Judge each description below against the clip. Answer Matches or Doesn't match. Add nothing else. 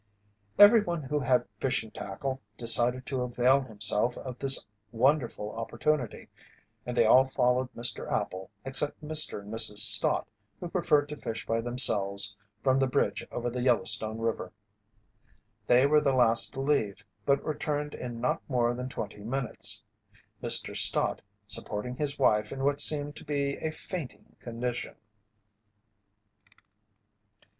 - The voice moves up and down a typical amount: Matches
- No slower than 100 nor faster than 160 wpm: Matches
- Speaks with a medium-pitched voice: Doesn't match